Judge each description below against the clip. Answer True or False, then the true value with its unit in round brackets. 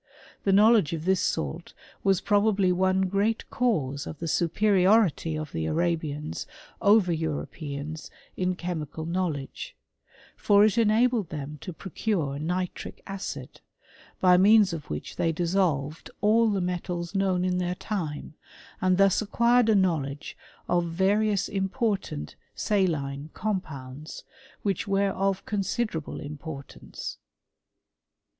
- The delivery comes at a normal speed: False (125 wpm)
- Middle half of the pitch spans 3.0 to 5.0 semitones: True (4.3 semitones)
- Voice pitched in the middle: True (180 Hz)